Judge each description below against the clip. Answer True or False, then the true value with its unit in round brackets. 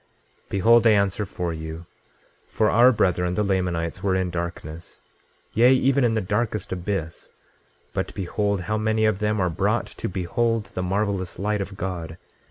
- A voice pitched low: True (100 Hz)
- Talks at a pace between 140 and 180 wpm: True (170 wpm)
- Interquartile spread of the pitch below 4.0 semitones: True (3.3 semitones)